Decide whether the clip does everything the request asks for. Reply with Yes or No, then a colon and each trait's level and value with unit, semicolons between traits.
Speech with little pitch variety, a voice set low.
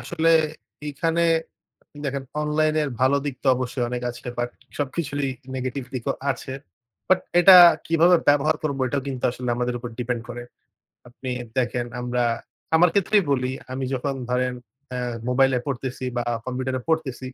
No: average, 3.2 semitones; low, 130 Hz